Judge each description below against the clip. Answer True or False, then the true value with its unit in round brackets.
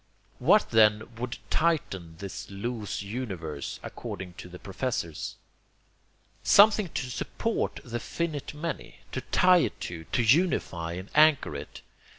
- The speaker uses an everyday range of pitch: False (8.6 semitones)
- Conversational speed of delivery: False (130 wpm)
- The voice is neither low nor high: False (115 Hz)